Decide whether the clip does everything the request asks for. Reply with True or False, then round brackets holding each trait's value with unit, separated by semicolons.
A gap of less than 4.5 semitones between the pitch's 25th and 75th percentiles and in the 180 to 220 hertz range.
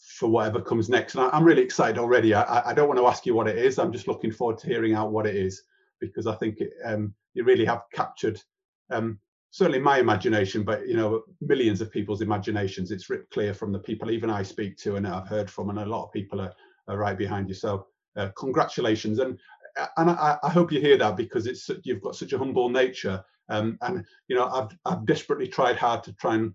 False (4.0 semitones; 110 Hz)